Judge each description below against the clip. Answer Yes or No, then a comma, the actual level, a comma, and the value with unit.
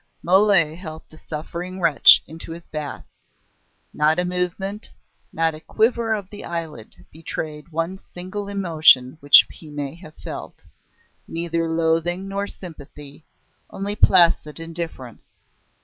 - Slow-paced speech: Yes, slow, 125 wpm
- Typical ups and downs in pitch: Yes, average, 3.0 semitones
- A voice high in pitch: No, medium, 165 Hz